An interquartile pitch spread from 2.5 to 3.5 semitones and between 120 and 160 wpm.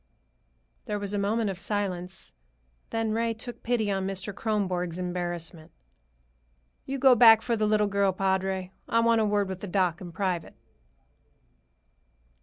Yes: average, 3.1 semitones; average, 150 wpm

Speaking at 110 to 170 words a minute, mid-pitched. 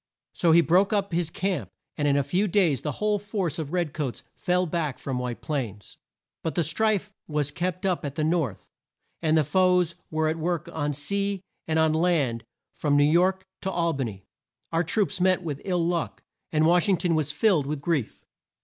No: fast, 205 wpm; medium, 165 Hz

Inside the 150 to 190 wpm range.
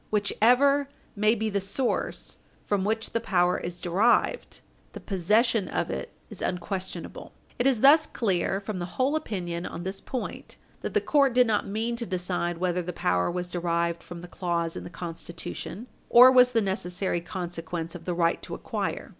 Yes: average, 180 wpm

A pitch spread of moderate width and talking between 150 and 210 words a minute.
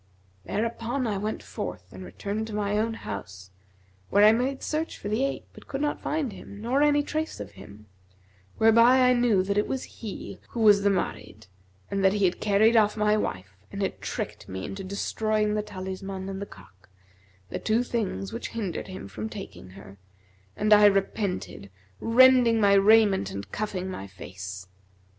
Yes: average, 3.5 semitones; average, 180 wpm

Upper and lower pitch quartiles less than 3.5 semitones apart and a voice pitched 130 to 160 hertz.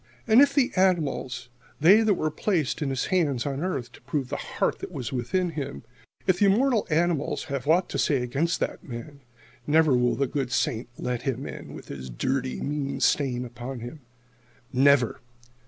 No: wide, 5.4 semitones; medium, 140 Hz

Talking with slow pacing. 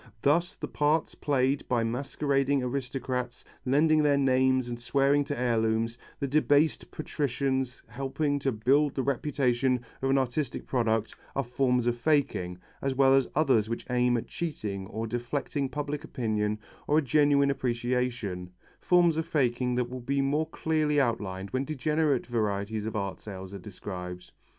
No: average, 155 wpm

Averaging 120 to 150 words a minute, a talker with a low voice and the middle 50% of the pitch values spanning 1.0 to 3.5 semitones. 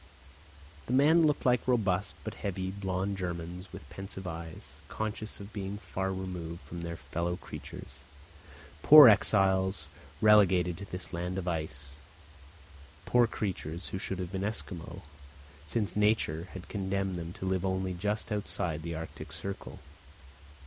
Yes: average, 140 wpm; very low, 95 Hz; average, 2.9 semitones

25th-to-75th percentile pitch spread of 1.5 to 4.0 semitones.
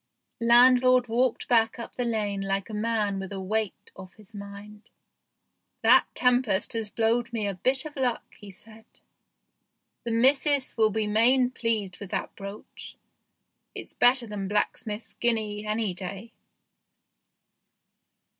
Yes: average, 2.9 semitones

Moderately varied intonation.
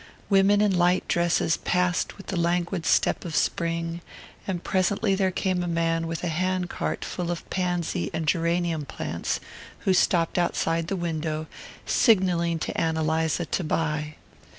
No: narrow, 1.9 semitones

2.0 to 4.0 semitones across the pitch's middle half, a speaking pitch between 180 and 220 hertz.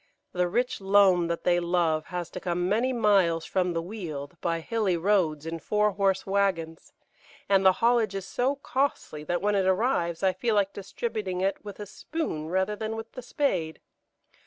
Yes: average, 3.4 semitones; high, 190 Hz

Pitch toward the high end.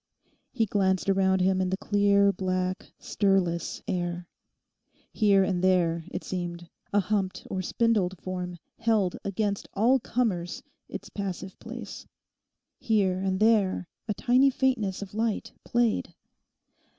Yes: high, 195 Hz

